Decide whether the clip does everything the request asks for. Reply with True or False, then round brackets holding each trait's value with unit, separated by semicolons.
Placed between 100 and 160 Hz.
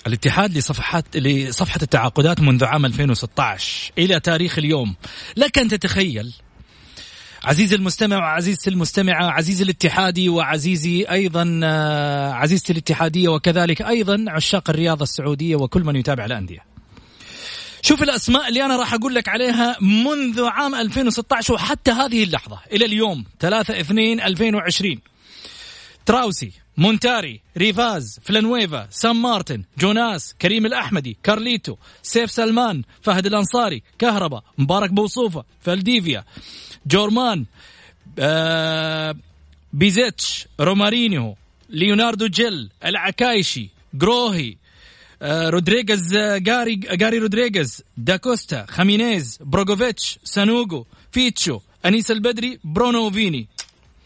False (185 Hz)